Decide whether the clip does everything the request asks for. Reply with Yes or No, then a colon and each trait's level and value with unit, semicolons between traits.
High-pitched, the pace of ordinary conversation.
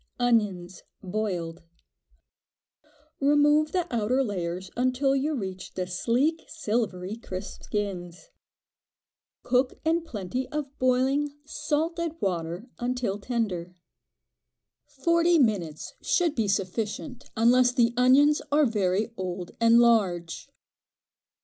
No: high, 235 Hz; slow, 100 wpm